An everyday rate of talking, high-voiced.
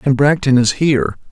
No: average, 185 wpm; low, 135 Hz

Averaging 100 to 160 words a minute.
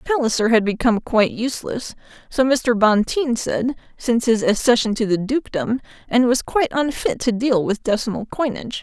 Yes: average, 150 wpm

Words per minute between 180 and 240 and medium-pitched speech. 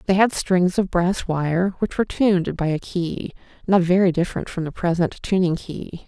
Yes: average, 200 wpm; medium, 180 Hz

